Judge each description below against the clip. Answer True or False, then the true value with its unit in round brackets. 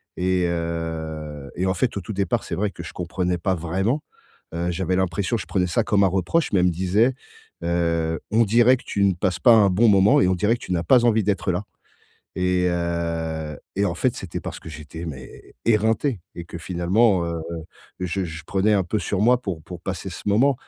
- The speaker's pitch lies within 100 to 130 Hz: False (90 Hz)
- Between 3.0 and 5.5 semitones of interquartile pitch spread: True (3.5 semitones)